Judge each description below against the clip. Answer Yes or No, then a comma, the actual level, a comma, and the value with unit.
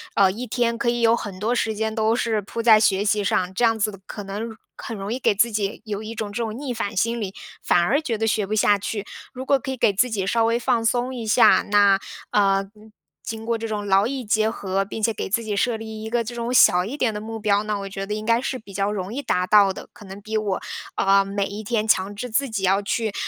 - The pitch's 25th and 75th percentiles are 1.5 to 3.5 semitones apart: Yes, narrow, 2.4 semitones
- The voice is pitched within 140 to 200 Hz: No, high, 215 Hz